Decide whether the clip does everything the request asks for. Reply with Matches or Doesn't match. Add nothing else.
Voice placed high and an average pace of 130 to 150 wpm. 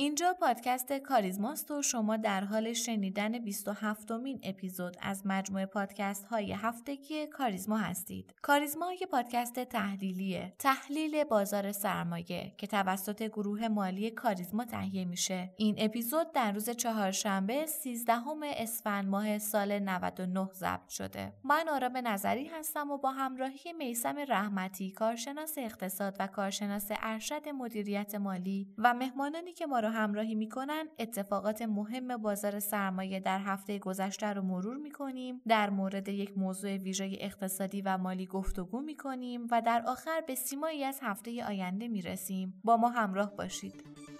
Matches